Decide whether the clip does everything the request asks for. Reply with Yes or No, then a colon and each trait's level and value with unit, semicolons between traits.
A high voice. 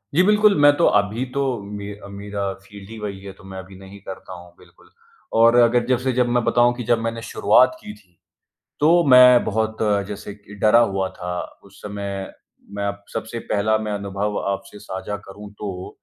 No: low, 105 Hz